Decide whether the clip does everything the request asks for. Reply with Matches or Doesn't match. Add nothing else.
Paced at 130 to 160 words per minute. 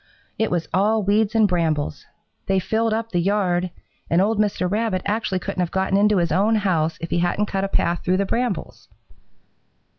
Doesn't match